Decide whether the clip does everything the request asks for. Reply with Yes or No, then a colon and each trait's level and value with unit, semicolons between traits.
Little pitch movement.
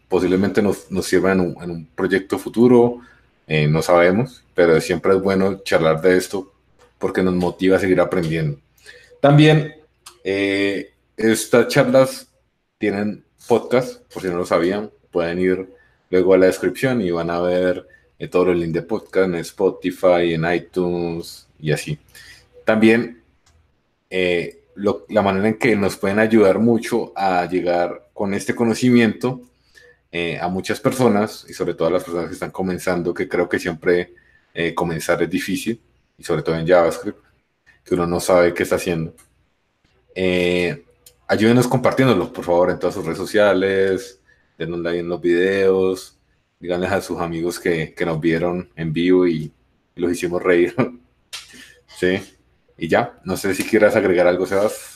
No: average, 4.1 semitones